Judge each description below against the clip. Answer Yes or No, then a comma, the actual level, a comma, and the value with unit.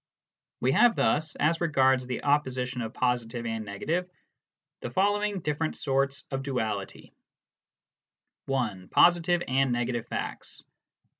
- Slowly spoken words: Yes, slow, 120 wpm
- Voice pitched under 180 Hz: Yes, low, 135 Hz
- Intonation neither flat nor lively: Yes, average, 4.6 semitones